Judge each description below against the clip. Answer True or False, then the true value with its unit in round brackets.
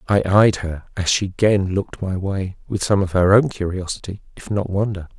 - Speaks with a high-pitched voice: False (95 Hz)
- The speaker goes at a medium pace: False (210 wpm)